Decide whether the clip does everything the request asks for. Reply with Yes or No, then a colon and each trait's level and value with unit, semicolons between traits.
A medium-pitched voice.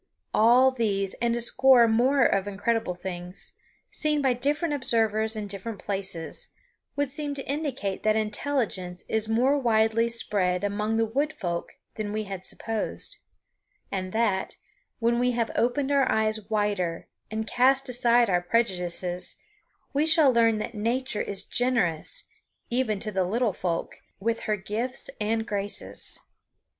No: high, 225 Hz